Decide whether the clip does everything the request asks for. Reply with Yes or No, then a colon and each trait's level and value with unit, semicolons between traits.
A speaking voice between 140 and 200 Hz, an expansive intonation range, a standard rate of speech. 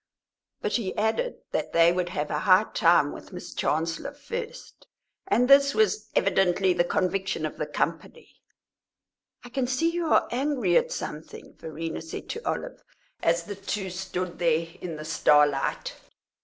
Yes: medium, 185 Hz; wide, 7.2 semitones; average, 155 wpm